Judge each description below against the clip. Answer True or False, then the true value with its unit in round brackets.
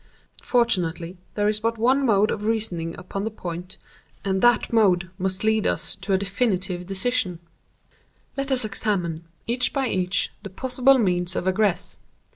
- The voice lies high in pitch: True (200 Hz)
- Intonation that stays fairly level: False (3.9 semitones)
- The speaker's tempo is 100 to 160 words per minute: True (155 wpm)